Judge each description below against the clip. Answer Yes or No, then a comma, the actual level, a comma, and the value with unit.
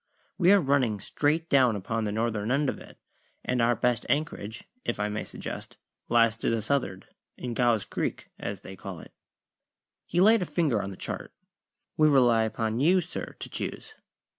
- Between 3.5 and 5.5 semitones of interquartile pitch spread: Yes, average, 5.2 semitones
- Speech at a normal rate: Yes, average, 185 wpm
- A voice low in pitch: Yes, low, 120 Hz